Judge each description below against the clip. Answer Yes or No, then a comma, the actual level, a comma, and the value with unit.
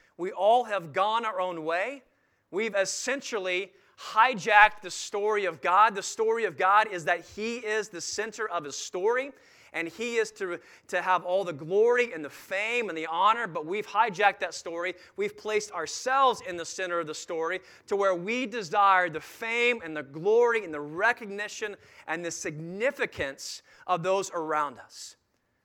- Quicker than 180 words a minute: No, average, 175 wpm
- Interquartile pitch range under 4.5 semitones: No, average, 5.1 semitones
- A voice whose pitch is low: No, high, 200 Hz